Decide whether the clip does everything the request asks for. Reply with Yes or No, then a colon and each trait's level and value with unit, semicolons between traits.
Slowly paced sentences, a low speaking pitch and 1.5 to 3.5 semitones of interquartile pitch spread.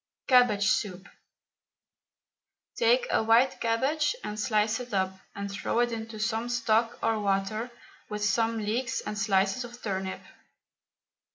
No: slow, 130 wpm; high, 220 Hz; average, 2.9 semitones